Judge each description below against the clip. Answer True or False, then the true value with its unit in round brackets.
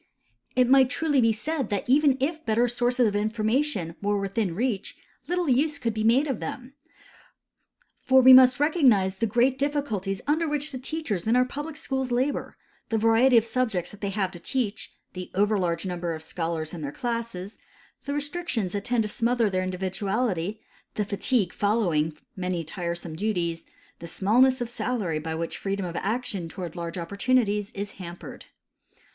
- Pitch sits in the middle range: False (220 Hz)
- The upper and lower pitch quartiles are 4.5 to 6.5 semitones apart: True (5.6 semitones)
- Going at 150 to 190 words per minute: True (170 wpm)